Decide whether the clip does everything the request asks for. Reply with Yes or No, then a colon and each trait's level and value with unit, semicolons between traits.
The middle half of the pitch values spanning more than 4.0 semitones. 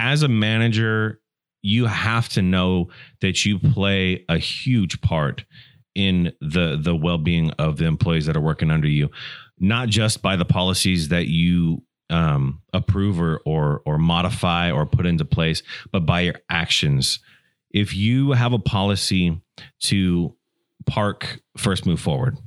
Yes: average, 4.8 semitones